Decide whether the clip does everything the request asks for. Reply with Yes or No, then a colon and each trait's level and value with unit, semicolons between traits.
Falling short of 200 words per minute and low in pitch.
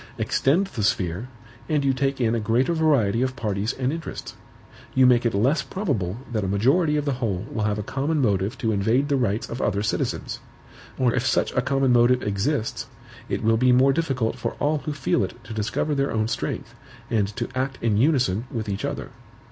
No: fast, 205 wpm; low, 125 Hz